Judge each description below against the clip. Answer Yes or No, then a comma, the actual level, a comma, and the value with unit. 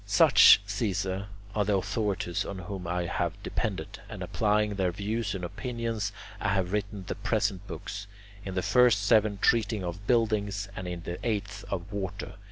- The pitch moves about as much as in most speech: No, narrow, 2.2 semitones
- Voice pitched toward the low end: Yes, low, 100 Hz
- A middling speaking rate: Yes, average, 170 wpm